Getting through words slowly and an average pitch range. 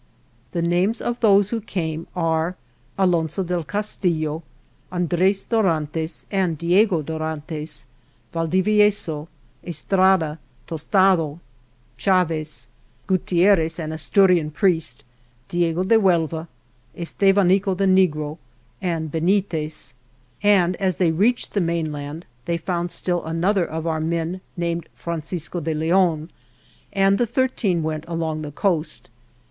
Yes: slow, 110 wpm; average, 3.1 semitones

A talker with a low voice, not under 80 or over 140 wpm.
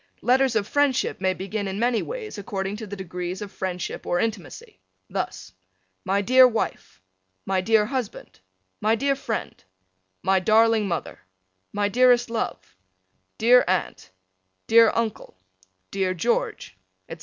No: high, 215 Hz; slow, 135 wpm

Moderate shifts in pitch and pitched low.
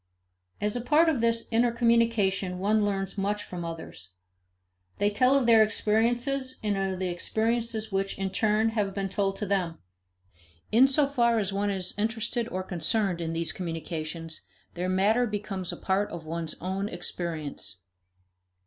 No: average, 3.8 semitones; high, 200 Hz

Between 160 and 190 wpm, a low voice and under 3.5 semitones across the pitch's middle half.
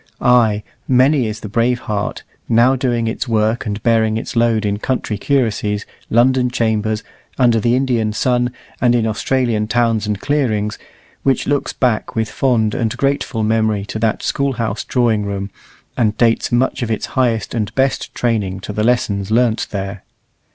Yes: average, 165 wpm; low, 115 Hz; narrow, 2.5 semitones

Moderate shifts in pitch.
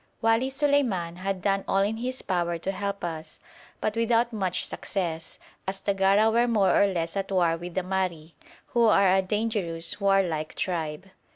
Yes: average, 3.9 semitones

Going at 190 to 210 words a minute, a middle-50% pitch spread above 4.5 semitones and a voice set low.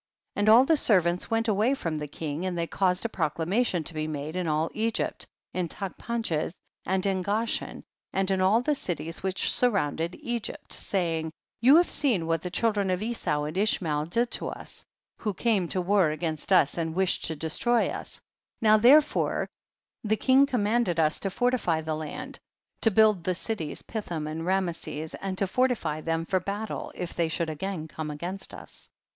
No: average, 200 wpm; average, 5.1 semitones; medium, 185 Hz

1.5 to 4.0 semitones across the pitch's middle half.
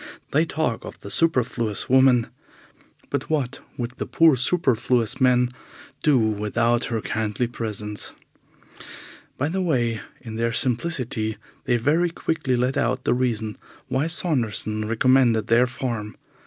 Yes: average, 2.9 semitones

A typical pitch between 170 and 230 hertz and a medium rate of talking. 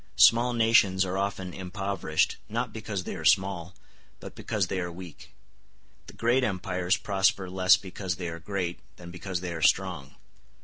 No: very low, 95 Hz; average, 165 wpm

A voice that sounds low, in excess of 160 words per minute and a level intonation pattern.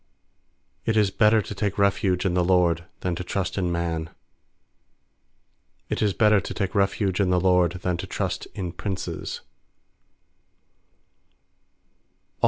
No: very low, 95 Hz; slow, 135 wpm; narrow, 2.2 semitones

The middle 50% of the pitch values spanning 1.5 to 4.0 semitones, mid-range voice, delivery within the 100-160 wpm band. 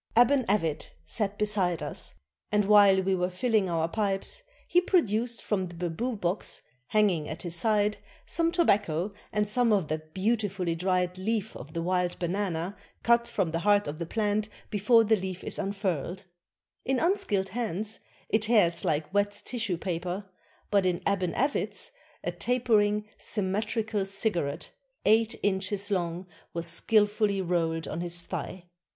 No: average, 3.5 semitones; high, 200 Hz; average, 155 wpm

